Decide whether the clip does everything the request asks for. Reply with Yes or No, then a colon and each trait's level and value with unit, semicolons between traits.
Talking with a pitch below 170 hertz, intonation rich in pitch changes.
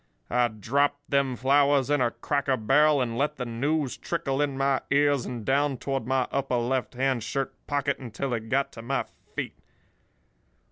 No: low, 135 Hz; narrow, 2.5 semitones